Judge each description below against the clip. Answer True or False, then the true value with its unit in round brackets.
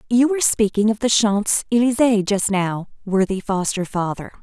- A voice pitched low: False (210 Hz)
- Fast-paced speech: False (165 wpm)